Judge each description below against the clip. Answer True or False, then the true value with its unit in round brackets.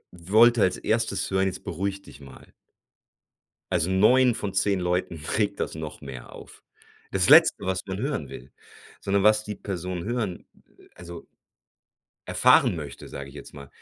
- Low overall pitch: True (95 Hz)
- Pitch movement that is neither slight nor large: True (3.4 semitones)